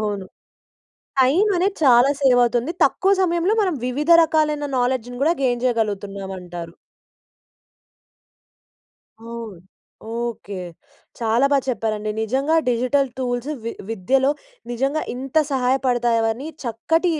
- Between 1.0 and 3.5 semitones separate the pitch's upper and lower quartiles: No, average, 3.9 semitones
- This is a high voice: Yes, high, 245 Hz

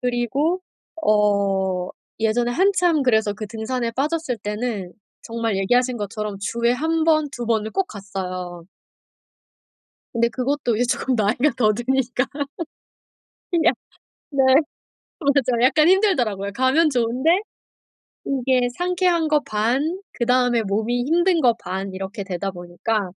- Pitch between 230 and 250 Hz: Yes, high, 240 Hz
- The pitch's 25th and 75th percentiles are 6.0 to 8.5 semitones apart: No, average, 5.2 semitones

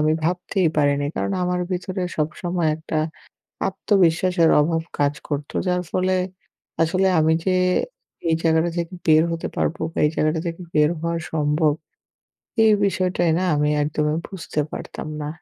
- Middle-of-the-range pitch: Yes, medium, 165 Hz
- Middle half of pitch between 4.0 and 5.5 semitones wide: No, average, 2.9 semitones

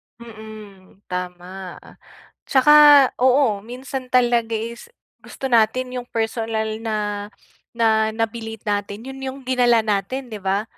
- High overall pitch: Yes, high, 225 Hz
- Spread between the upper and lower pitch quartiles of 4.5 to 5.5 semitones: No, average, 3.1 semitones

